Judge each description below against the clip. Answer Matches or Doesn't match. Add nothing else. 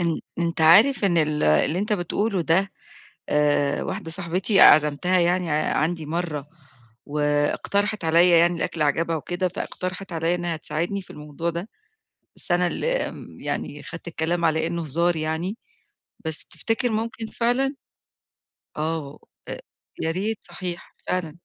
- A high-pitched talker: Doesn't match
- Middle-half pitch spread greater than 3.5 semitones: Doesn't match